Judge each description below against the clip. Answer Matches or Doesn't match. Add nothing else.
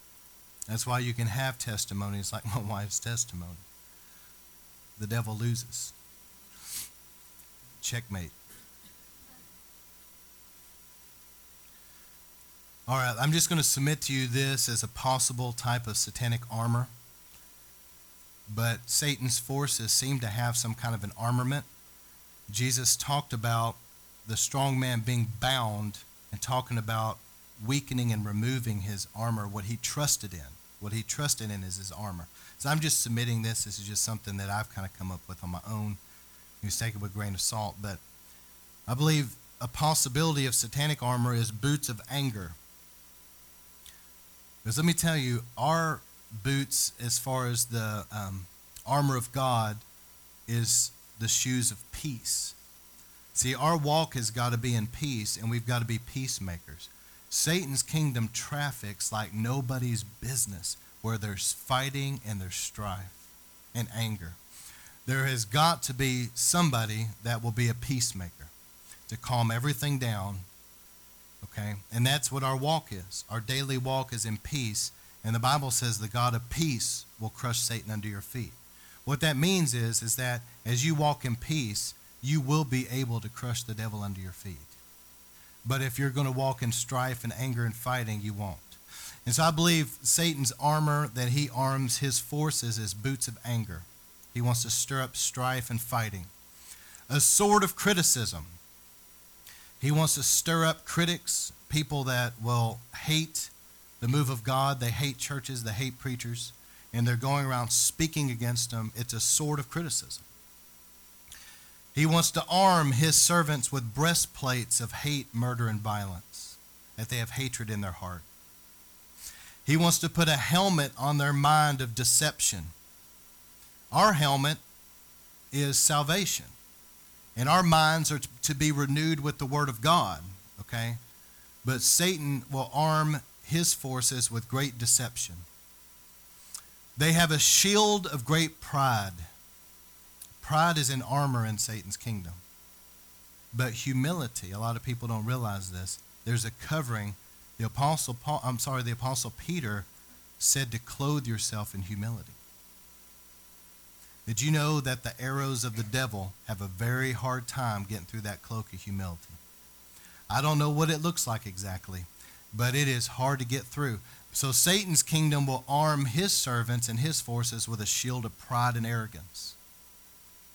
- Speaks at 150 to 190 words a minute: Matches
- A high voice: Doesn't match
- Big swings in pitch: Matches